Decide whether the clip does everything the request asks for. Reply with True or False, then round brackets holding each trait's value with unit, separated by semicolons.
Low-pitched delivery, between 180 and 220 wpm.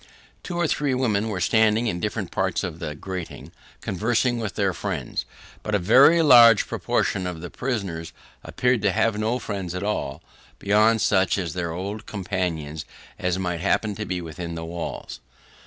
False (100 Hz; 170 wpm)